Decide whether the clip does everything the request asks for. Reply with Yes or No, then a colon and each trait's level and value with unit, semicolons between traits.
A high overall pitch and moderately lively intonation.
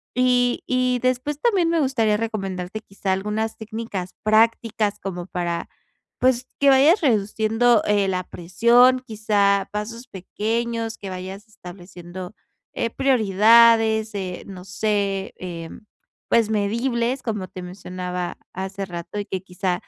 Yes: high, 215 Hz; average, 3.7 semitones